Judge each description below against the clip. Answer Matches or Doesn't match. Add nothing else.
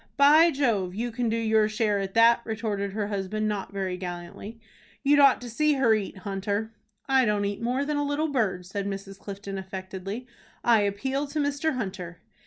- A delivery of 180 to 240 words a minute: Matches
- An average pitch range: Matches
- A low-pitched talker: Doesn't match